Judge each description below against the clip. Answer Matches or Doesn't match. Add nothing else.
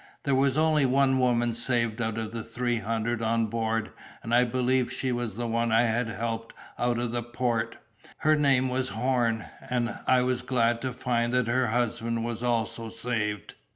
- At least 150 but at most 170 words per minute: Doesn't match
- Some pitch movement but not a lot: Doesn't match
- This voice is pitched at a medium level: Doesn't match